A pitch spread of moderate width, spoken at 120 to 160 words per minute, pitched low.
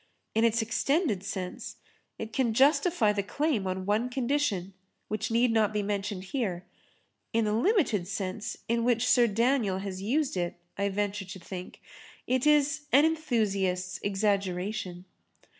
No: average, 4.4 semitones; average, 145 wpm; high, 215 Hz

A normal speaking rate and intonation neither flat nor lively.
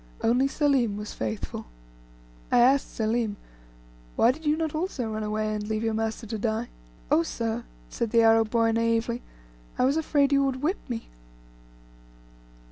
Yes: average, 160 wpm; average, 3.6 semitones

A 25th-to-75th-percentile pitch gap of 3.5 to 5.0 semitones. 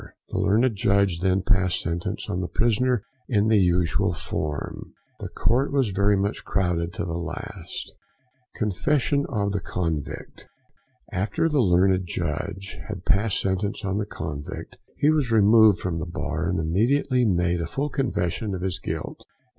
Yes: average, 4.1 semitones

